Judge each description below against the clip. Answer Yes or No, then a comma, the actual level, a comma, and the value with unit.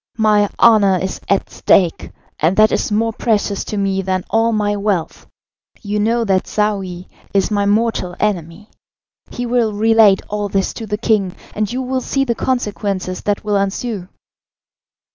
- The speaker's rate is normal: Yes, average, 160 wpm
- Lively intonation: No, narrow, 2.4 semitones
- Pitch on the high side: Yes, high, 210 Hz